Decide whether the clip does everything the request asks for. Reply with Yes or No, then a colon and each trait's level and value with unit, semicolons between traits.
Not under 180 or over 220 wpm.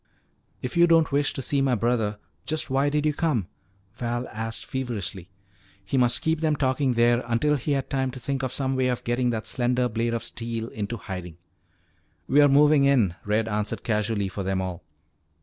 Yes: average, 190 wpm